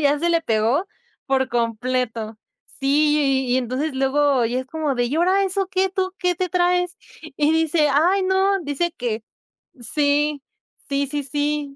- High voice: Yes, very high, 290 Hz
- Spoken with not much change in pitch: No, average, 4.6 semitones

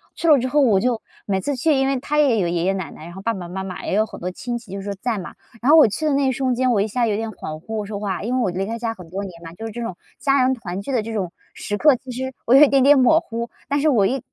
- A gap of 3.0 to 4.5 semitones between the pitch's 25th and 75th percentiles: No, average, 5.2 semitones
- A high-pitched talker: Yes, high, 230 Hz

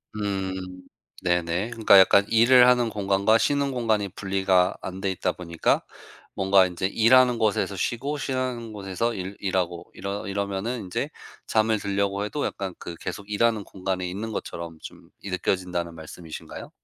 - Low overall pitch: Yes, low, 100 Hz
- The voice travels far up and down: No, average, 3.4 semitones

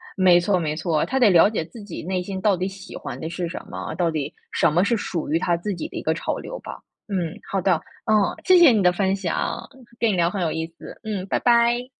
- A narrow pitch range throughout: No, average, 3.6 semitones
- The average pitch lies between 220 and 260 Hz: No, medium, 185 Hz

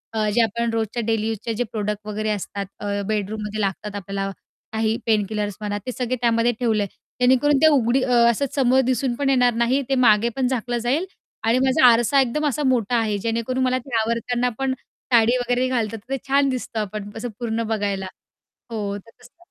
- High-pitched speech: Yes, high, 230 Hz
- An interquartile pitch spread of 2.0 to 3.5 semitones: Yes, average, 2.9 semitones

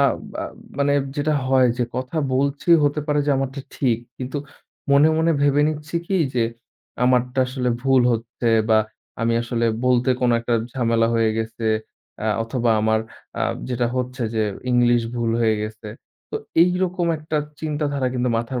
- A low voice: Yes, low, 125 Hz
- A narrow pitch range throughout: No, average, 3.5 semitones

